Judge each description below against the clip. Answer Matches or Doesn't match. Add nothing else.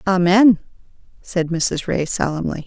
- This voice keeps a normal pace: Doesn't match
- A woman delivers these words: Matches